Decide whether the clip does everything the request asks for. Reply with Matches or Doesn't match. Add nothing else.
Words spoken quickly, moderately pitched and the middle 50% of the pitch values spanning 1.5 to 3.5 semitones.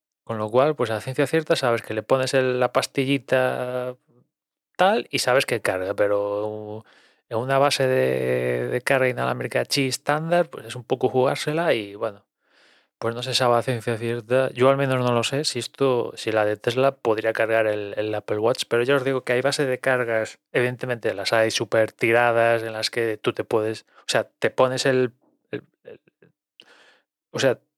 Doesn't match